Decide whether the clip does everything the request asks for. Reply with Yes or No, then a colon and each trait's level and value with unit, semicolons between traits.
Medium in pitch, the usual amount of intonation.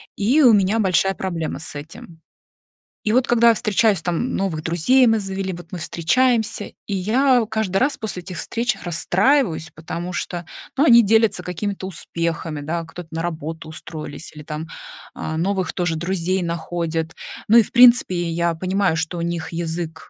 Yes: medium, 180 Hz; average, 4.6 semitones